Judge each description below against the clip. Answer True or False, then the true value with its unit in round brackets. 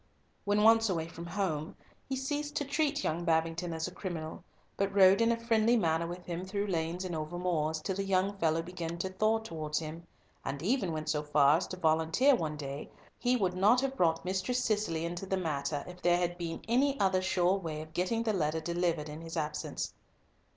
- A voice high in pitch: False (175 Hz)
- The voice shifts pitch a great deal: False (4.1 semitones)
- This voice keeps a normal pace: False (215 wpm)